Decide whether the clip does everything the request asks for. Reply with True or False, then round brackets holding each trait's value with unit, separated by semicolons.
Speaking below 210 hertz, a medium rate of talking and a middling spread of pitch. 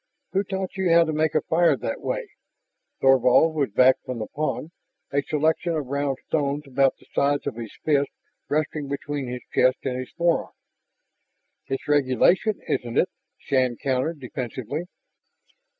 True (140 Hz; 155 wpm; 3.6 semitones)